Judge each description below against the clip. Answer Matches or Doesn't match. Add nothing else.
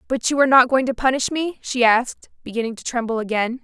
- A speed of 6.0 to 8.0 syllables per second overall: Matches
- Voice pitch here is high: Matches